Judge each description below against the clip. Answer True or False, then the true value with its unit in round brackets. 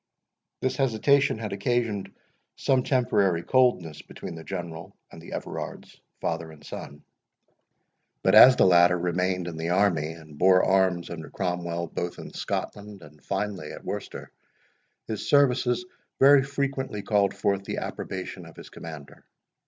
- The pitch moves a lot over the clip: True (5.7 semitones)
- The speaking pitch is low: True (95 Hz)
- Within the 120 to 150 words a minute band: True (145 wpm)